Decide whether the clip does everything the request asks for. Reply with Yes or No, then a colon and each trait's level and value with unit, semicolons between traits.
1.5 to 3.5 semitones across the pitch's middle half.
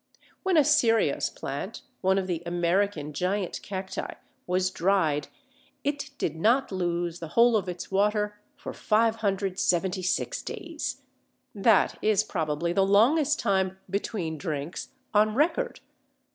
No: average, 4.3 semitones